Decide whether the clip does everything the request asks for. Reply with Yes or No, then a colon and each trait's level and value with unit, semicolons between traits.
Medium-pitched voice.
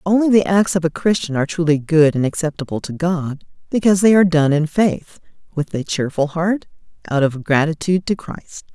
Yes: medium, 165 Hz